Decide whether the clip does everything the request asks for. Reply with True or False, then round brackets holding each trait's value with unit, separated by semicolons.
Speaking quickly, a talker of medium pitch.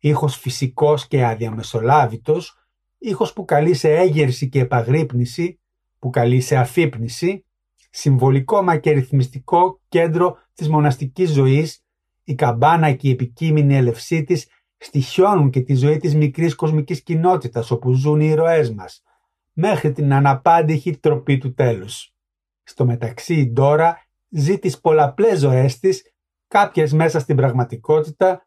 False (130 wpm; 150 Hz)